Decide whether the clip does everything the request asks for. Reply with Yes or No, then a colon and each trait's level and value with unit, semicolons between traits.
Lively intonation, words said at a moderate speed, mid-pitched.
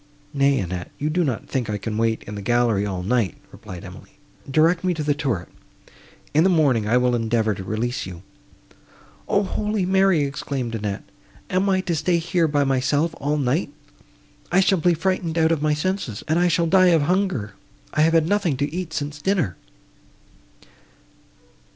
Yes: wide, 7.0 semitones; average, 180 wpm; medium, 145 Hz